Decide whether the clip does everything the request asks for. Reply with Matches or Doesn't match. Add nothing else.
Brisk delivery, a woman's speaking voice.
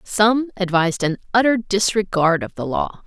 Doesn't match